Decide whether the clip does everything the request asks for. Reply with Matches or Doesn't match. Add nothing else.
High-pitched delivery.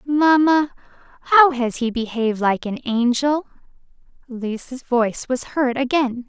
Matches